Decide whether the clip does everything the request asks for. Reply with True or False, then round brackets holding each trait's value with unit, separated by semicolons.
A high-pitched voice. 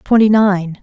True (200 Hz)